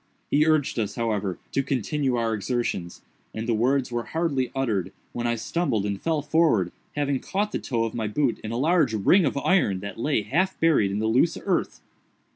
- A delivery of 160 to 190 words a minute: No, average, 200 wpm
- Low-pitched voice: Yes, low, 120 Hz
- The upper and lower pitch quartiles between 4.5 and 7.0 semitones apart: Yes, average, 5.3 semitones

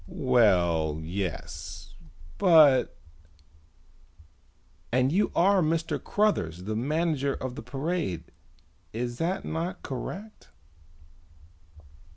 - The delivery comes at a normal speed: No, slow, 90 wpm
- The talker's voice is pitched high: No, low, 125 Hz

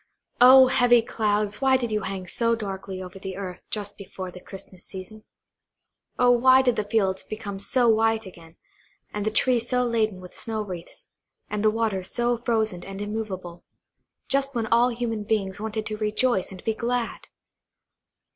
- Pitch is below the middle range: No, high, 215 Hz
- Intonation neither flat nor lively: Yes, average, 3.5 semitones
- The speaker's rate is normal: Yes, average, 170 wpm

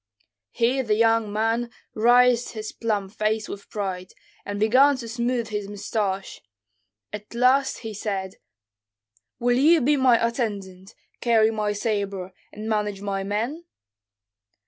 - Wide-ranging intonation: No, average, 2.8 semitones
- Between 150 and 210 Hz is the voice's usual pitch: No, high, 220 Hz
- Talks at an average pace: No, slow, 130 wpm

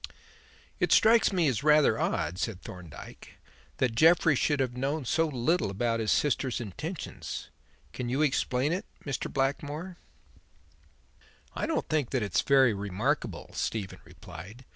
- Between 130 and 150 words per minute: Yes, average, 140 wpm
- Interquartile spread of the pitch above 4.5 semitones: Yes, average, 5.0 semitones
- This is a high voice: No, low, 135 Hz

